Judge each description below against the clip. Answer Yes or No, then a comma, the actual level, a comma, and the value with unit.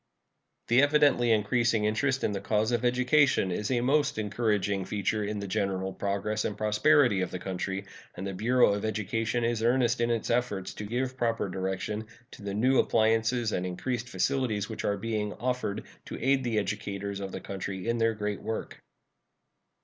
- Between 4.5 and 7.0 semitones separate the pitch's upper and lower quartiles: No, average, 3.2 semitones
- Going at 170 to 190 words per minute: Yes, average, 180 wpm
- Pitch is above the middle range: No, low, 110 Hz